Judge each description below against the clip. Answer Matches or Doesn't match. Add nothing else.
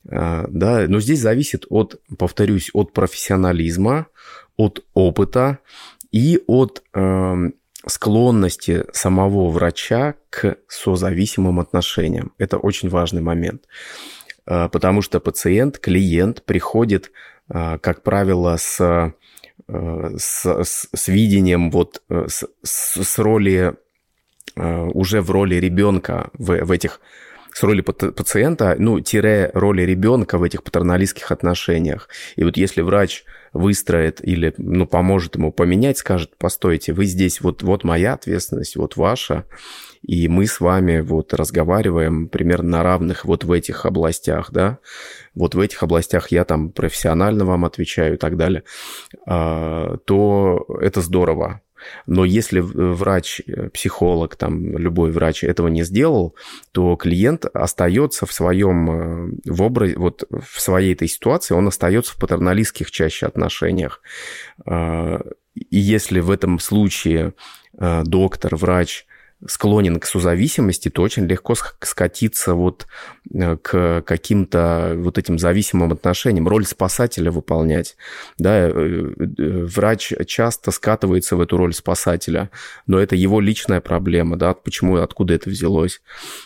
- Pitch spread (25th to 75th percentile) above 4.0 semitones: Doesn't match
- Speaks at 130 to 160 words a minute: Doesn't match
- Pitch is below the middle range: Matches